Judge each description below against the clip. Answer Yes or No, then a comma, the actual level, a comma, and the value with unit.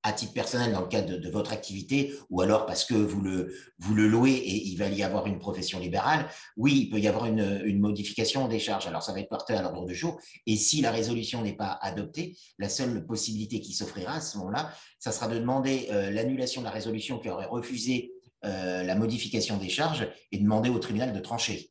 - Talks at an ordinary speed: No, fast, 230 wpm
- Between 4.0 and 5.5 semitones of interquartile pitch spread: No, average, 3.2 semitones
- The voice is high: No, low, 110 Hz